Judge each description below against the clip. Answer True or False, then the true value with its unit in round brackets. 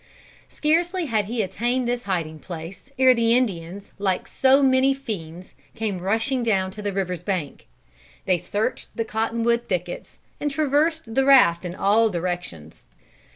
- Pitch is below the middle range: False (220 Hz)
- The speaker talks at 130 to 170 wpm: True (155 wpm)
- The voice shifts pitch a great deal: True (6.0 semitones)